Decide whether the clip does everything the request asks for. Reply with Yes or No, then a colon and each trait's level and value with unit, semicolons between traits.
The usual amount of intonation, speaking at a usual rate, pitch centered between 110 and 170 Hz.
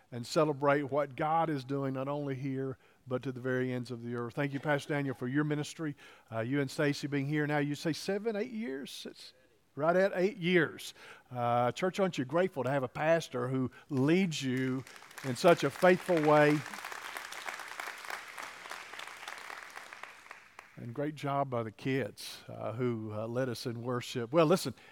Yes: average, 3.4 semitones; average, 175 wpm; medium, 140 Hz